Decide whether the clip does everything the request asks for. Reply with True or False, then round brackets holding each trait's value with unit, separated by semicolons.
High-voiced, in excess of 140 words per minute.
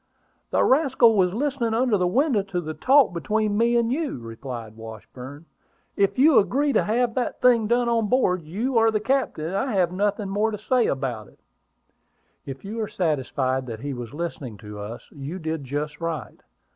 True (195 Hz; 190 wpm)